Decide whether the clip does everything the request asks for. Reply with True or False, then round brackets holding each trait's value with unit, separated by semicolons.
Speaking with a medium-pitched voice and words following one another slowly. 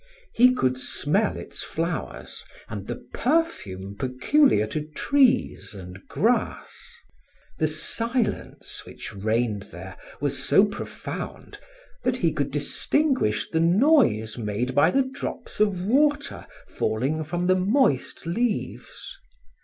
True (165 Hz; 115 wpm)